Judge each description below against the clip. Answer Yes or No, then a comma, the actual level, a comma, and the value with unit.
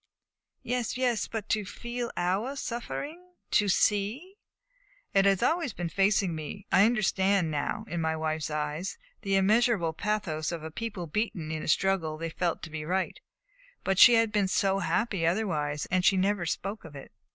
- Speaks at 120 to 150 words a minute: No, average, 175 wpm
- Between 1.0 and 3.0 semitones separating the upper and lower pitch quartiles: No, average, 5.2 semitones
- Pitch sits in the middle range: No, high, 195 Hz